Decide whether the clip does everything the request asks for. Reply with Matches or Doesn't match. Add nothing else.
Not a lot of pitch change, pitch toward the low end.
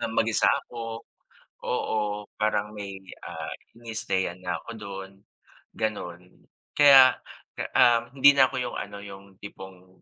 Doesn't match